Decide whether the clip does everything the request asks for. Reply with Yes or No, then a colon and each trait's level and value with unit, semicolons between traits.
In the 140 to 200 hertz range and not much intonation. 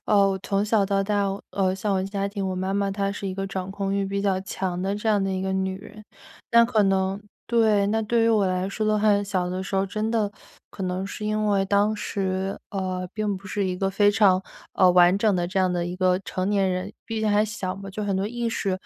Yes: high, 195 Hz; narrow, 1.7 semitones